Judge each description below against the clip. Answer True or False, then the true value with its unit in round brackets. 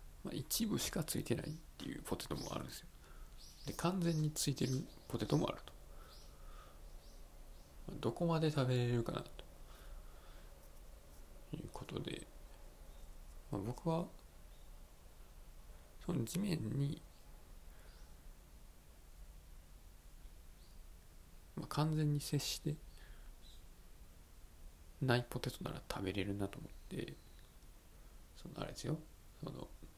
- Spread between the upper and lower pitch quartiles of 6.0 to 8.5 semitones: False (5.3 semitones)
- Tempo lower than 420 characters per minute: True (180 characters per minute)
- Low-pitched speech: True (80 Hz)